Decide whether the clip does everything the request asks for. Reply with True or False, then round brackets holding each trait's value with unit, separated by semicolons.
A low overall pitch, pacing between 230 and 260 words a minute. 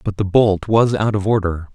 True (100 Hz; 240 wpm)